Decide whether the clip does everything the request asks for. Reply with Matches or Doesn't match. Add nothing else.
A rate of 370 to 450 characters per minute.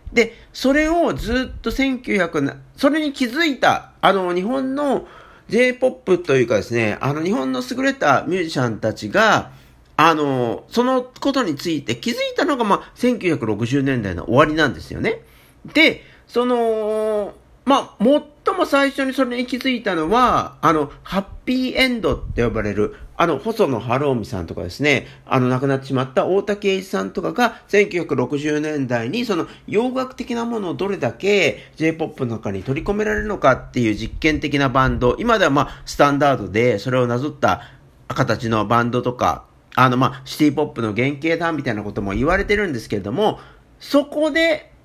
Doesn't match